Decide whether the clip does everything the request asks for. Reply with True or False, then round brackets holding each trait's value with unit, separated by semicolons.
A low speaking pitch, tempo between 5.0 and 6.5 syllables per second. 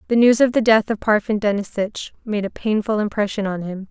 False (210 Hz; 5.6 syllables/s)